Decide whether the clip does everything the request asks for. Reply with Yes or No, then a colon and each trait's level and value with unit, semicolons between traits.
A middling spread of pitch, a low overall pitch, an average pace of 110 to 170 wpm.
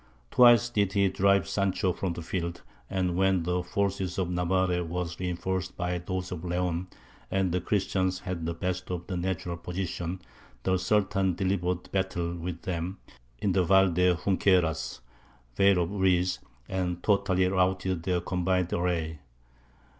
No: narrow, 1.4 semitones; very low, 90 Hz; average, 150 wpm